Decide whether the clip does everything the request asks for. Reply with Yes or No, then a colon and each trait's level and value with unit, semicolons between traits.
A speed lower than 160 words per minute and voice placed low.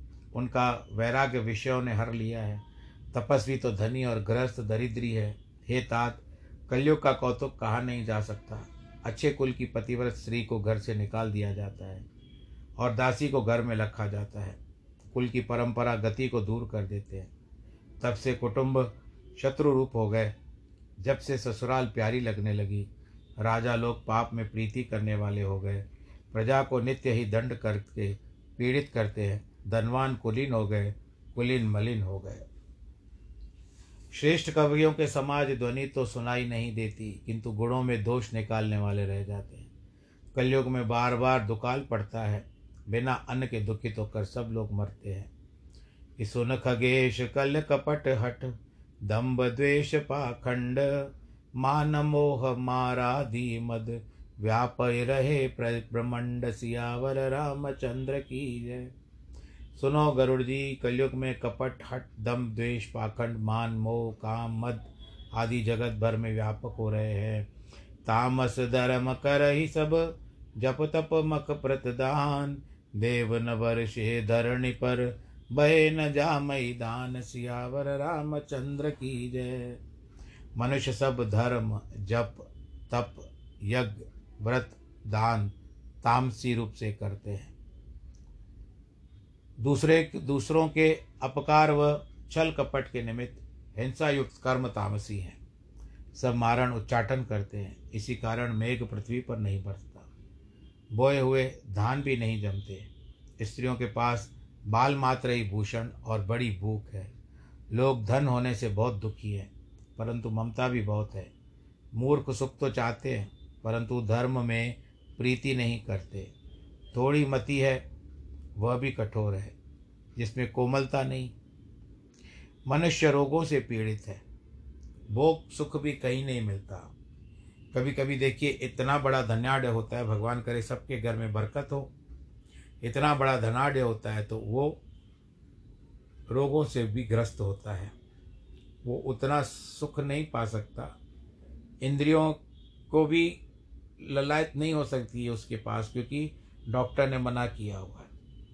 Yes: average, 140 wpm; low, 120 Hz